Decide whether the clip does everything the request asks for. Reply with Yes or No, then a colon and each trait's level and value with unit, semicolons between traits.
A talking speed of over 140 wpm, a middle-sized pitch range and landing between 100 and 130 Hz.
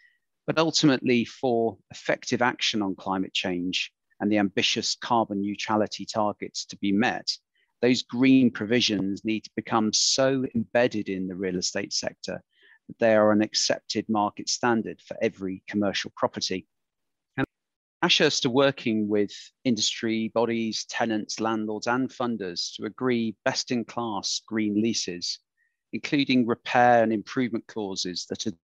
No: slow, 135 wpm; average, 3.1 semitones; low, 110 Hz